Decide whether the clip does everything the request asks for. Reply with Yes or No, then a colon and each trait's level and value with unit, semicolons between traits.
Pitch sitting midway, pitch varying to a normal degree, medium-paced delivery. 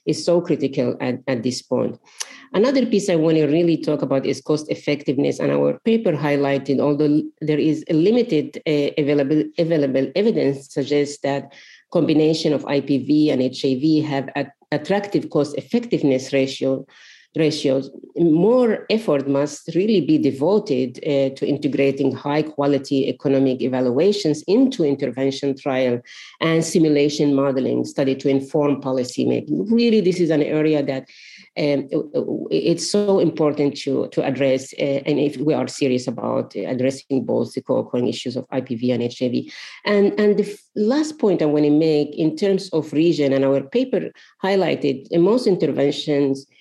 Yes: medium, 145 Hz; average, 3.1 semitones; average, 155 wpm